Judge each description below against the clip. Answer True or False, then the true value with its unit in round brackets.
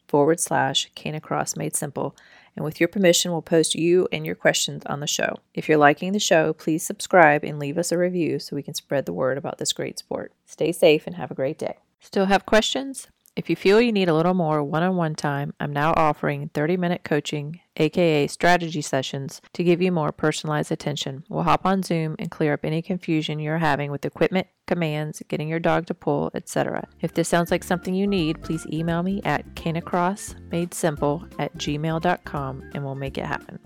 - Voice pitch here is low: False (165 Hz)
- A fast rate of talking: True (210 wpm)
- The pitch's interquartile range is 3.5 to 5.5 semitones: False (2.9 semitones)